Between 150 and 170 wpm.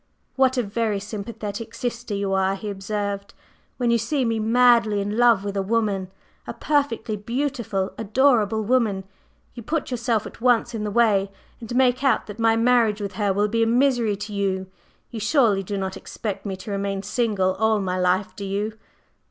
No: average, 185 wpm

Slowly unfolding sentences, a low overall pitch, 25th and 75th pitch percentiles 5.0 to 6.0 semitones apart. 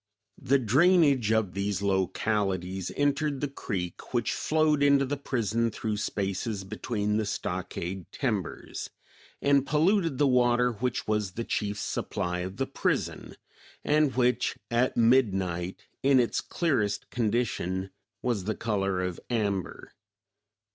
Yes: slow, 125 wpm; low, 110 Hz; wide, 5.4 semitones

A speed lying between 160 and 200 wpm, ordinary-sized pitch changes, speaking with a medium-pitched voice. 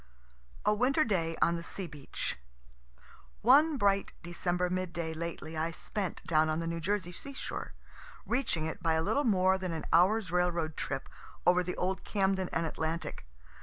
Yes: average, 170 wpm; average, 3.2 semitones; medium, 180 Hz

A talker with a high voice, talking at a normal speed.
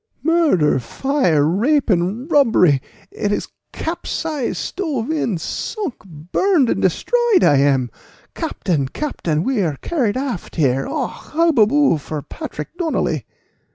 No: high, 230 Hz; slow, 120 wpm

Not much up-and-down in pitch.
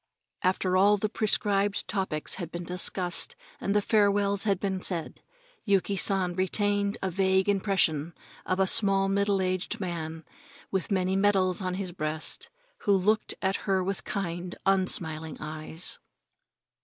Yes: narrow, 2.0 semitones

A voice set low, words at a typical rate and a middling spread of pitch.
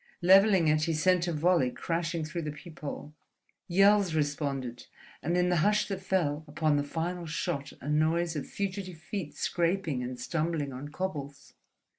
No: medium, 160 Hz; average, 160 wpm; average, 3.5 semitones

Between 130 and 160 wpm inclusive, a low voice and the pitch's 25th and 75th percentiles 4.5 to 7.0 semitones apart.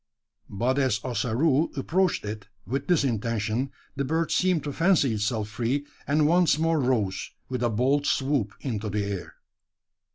Yes: average, 155 wpm; low, 130 Hz; average, 5.3 semitones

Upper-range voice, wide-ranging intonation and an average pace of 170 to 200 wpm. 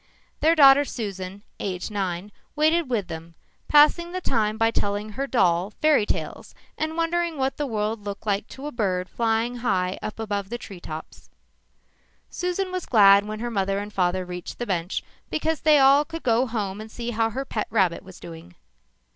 Yes: high, 220 Hz; wide, 5.9 semitones; average, 190 wpm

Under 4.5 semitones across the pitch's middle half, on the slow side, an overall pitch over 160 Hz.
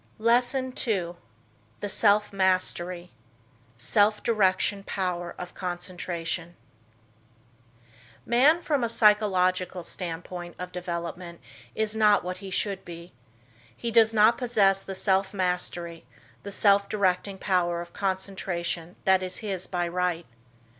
Yes: average, 2.9 semitones; slow, 120 wpm; high, 190 Hz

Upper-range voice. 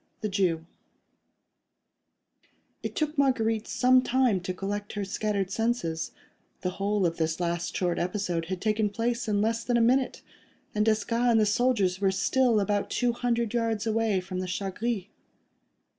Yes: high, 210 Hz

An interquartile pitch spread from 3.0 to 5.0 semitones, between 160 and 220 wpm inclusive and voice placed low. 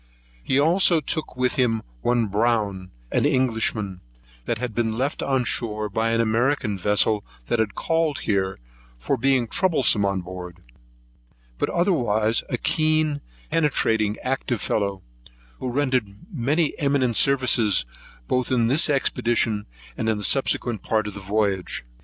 No: average, 4.6 semitones; average, 140 wpm; low, 115 Hz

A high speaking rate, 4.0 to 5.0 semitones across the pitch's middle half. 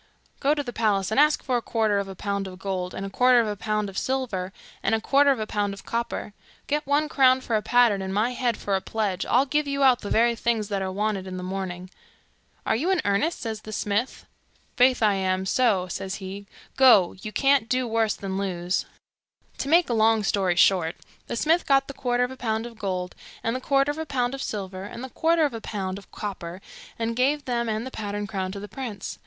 Yes: fast, 240 wpm; average, 4.6 semitones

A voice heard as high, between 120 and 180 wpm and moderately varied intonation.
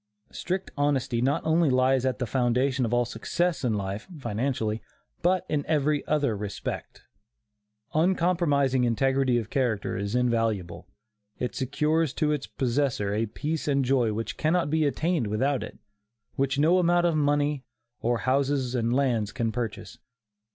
No: low, 135 Hz; average, 150 wpm; average, 4.1 semitones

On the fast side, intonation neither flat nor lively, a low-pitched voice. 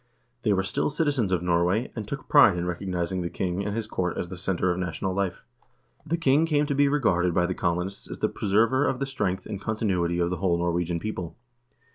Yes: fast, 220 wpm; average, 4.5 semitones; very low, 95 Hz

